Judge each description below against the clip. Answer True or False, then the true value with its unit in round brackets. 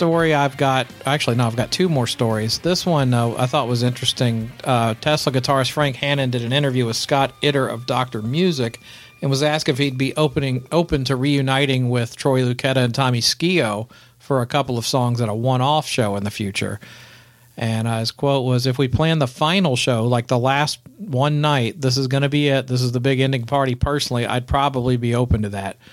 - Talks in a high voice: False (130 Hz)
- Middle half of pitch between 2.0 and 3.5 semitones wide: True (2.8 semitones)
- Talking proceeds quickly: True (220 wpm)